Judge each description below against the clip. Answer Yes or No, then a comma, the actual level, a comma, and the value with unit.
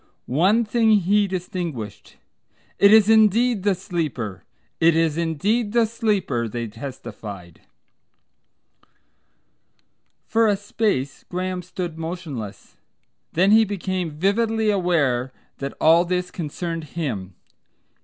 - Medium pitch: Yes, medium, 180 Hz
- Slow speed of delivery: Yes, slow, 105 wpm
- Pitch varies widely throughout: Yes, wide, 6.3 semitones